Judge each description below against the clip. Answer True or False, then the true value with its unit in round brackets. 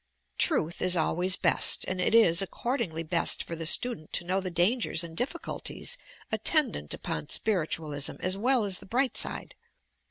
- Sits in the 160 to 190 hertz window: True (185 Hz)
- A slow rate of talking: False (160 wpm)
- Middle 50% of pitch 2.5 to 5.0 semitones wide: False (5.6 semitones)